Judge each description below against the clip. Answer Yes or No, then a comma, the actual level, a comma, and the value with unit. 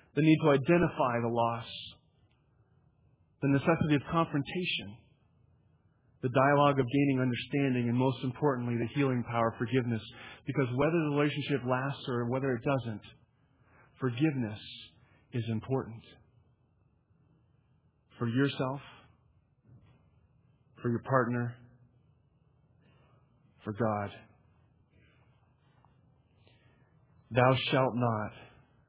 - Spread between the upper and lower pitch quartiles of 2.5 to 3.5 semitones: Yes, average, 2.8 semitones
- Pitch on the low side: Yes, low, 130 Hz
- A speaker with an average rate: No, slow, 95 wpm